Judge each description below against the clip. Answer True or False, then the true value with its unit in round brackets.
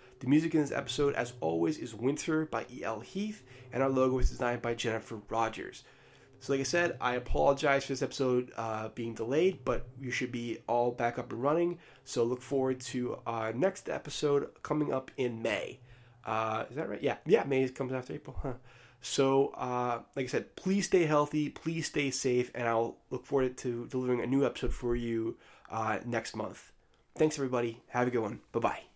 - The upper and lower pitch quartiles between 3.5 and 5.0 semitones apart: False (2.7 semitones)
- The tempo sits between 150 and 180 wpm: False (200 wpm)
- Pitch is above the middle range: False (125 Hz)